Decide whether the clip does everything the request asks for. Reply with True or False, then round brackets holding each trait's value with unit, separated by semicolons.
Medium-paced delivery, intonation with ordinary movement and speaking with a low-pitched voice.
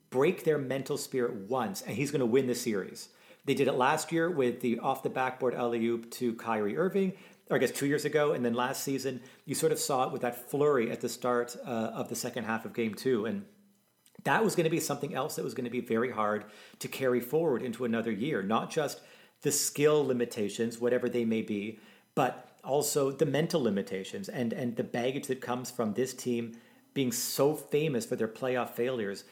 False (215 wpm; 3.6 semitones; 125 Hz)